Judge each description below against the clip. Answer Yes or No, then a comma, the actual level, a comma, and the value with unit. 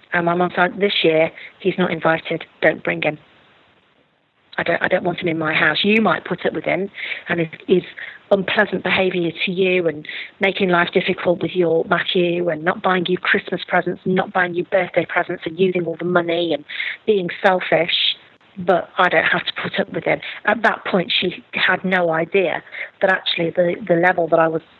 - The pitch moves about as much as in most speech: No, narrow, 1.9 semitones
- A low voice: No, medium, 180 Hz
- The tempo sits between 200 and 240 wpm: Yes, fast, 205 wpm